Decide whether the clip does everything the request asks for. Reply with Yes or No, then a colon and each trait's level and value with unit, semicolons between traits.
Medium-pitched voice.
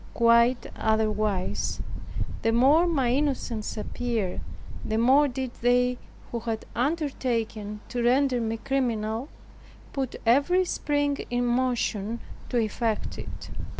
No: high, 240 Hz